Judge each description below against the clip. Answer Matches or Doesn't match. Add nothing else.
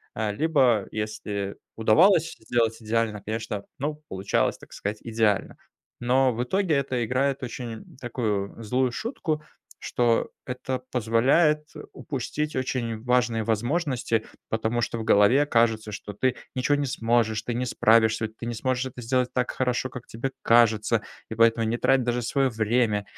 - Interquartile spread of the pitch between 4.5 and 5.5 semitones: Doesn't match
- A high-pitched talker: Doesn't match